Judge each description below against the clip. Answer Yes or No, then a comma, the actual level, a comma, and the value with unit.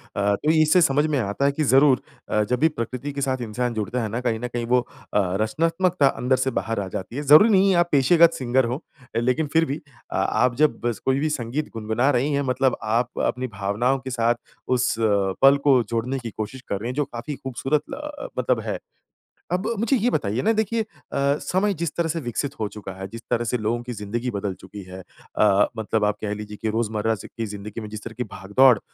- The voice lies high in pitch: No, low, 125 Hz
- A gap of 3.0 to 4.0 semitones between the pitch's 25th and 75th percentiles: No, average, 4.8 semitones